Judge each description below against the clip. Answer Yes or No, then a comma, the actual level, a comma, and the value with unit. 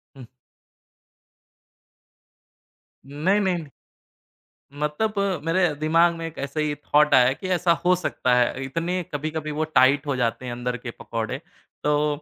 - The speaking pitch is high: No, medium, 150 Hz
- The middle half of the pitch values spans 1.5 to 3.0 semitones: No, average, 4.2 semitones